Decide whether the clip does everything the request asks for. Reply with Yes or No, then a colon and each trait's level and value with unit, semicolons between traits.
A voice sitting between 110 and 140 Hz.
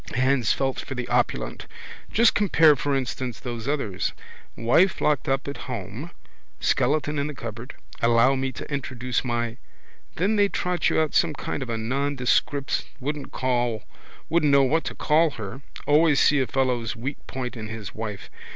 Yes: low, 135 Hz